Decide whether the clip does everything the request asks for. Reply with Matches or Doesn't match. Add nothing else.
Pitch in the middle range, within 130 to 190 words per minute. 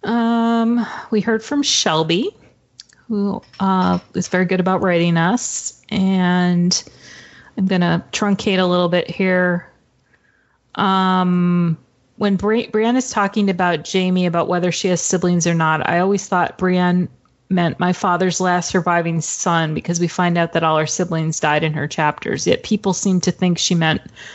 Matches